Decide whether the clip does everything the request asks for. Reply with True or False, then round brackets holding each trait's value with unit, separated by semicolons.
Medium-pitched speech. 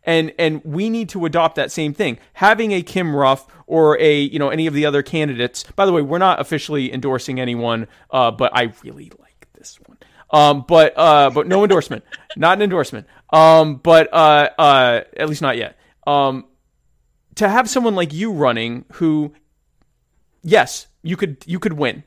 True (155 Hz)